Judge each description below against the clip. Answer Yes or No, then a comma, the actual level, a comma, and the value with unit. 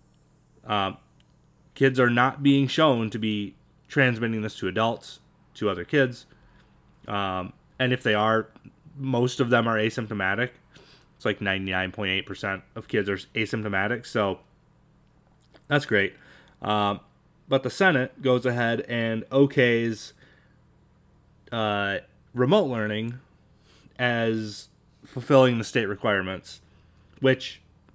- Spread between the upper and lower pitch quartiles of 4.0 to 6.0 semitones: Yes, average, 4.6 semitones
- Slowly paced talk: Yes, slow, 115 wpm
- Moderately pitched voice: No, low, 115 Hz